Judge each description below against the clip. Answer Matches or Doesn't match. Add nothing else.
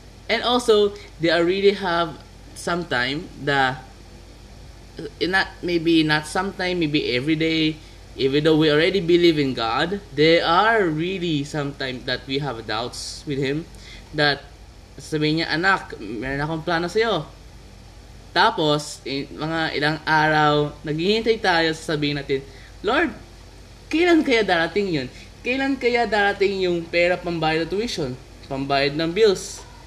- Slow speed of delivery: Doesn't match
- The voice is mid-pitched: Matches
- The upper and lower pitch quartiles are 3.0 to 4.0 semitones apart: Doesn't match